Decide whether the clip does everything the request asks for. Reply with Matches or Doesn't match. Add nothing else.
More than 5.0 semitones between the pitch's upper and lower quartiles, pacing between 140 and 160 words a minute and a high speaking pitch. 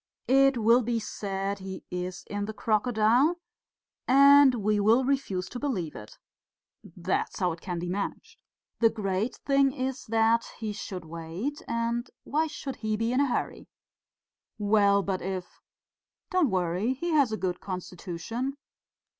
Matches